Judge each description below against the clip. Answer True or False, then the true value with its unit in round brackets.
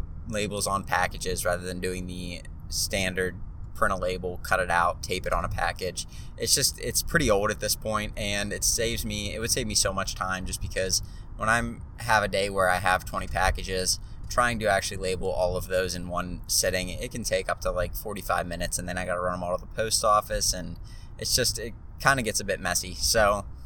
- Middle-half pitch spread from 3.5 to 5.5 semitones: False (2.7 semitones)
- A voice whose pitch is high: False (95 Hz)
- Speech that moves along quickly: True (230 wpm)